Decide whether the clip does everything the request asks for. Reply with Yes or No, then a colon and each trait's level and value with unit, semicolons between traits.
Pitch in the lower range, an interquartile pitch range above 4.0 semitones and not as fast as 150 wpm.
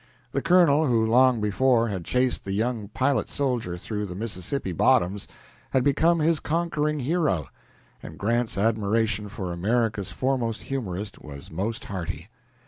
Yes: low, 115 Hz; average, 5.1 semitones; average, 140 wpm